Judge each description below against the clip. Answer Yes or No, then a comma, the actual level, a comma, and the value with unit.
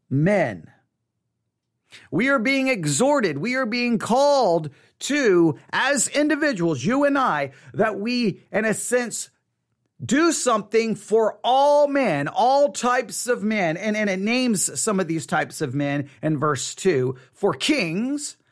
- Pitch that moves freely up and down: Yes, wide, 8.0 semitones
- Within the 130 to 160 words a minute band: Yes, average, 145 wpm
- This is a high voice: Yes, high, 215 Hz